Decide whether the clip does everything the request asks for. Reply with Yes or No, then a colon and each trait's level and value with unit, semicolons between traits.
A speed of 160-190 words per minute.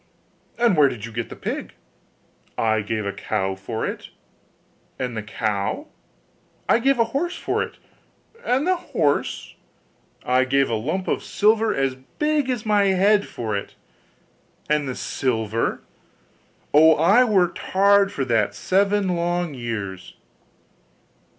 No: average, 140 wpm